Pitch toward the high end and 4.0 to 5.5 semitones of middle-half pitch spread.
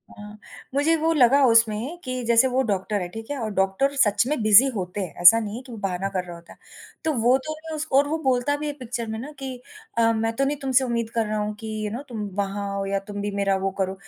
Yes: high, 230 Hz; average, 4.6 semitones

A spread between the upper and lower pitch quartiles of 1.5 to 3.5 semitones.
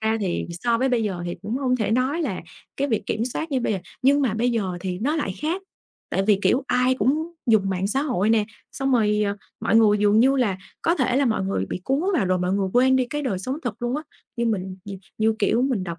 No: average, 4.6 semitones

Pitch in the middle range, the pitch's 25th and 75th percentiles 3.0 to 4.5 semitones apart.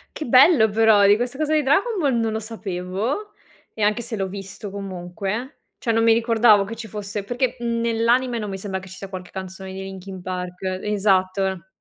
No: high, 210 Hz; average, 3.6 semitones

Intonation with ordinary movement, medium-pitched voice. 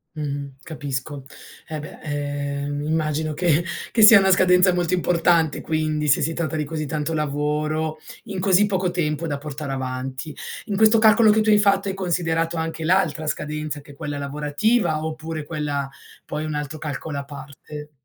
Yes: average, 3.1 semitones; medium, 155 Hz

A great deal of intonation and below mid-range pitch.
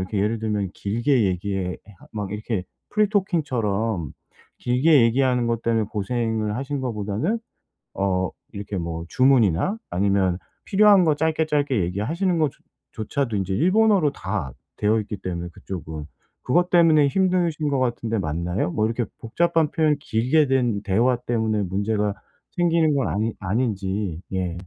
Yes: wide, 6.7 semitones; low, 115 Hz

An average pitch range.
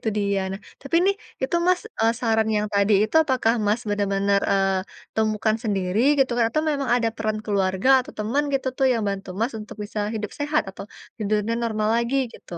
Yes: average, 3.5 semitones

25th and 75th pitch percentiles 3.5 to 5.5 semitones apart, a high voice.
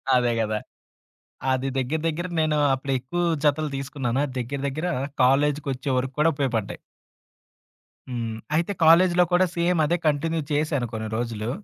No: average, 4.0 semitones; medium, 140 Hz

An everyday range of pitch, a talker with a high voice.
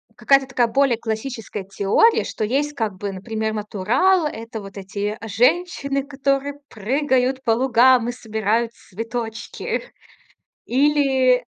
Yes: average, 3.9 semitones; high, 240 Hz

